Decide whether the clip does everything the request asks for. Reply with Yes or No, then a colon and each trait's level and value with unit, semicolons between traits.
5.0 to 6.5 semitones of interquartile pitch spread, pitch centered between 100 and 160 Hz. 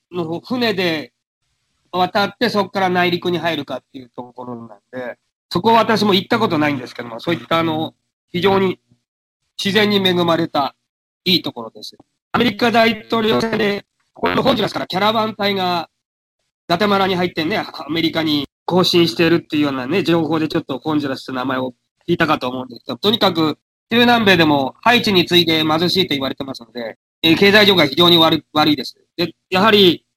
No: wide, 5.6 semitones; medium, 170 Hz